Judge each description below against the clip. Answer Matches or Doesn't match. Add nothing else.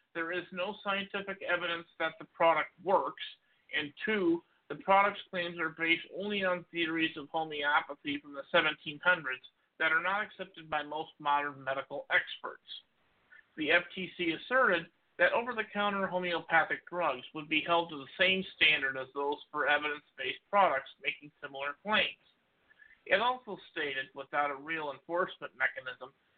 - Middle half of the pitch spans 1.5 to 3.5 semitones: Doesn't match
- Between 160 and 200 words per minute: Doesn't match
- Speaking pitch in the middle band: Matches